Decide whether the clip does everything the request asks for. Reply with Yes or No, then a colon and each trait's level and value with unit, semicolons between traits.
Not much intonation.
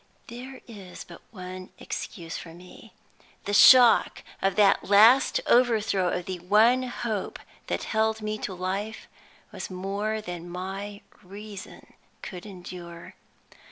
No: average, 3.1 semitones